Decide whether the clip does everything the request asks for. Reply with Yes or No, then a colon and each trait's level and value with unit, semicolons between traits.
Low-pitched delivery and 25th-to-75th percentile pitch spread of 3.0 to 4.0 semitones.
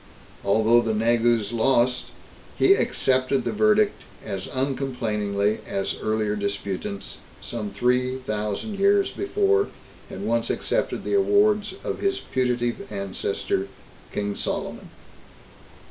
No: low, 120 Hz; average, 4.8 semitones